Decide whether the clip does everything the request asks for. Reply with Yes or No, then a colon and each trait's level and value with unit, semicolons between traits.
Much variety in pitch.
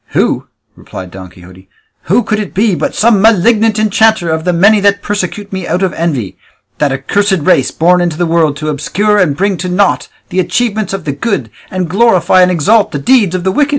No: average, 4.6 semitones